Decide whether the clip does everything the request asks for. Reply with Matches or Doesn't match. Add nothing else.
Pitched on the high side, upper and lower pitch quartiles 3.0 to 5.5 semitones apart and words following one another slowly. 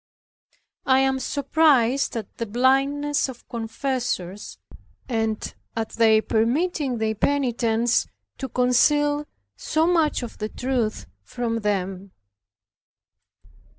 Matches